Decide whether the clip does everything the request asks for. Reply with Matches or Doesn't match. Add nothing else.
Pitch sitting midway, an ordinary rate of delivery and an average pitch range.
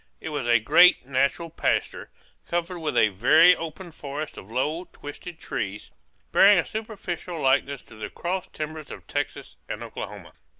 Matches